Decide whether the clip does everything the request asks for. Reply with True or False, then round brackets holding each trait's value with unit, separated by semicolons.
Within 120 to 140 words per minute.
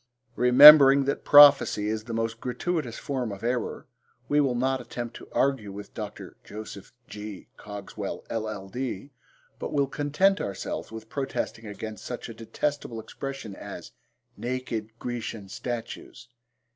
True (135 wpm)